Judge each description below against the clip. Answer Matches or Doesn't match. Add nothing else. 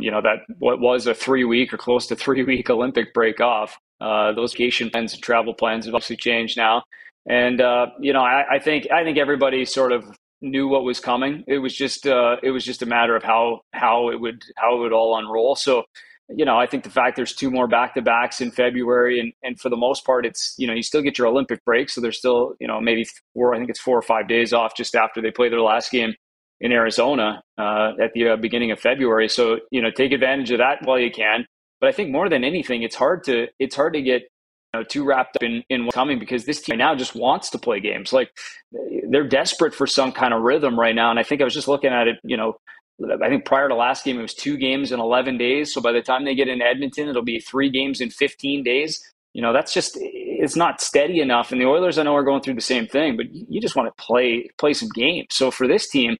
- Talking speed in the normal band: Doesn't match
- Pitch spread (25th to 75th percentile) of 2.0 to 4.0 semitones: Matches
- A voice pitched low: Matches